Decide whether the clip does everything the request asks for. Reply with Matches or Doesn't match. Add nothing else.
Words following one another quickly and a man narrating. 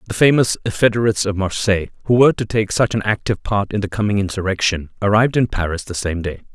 Matches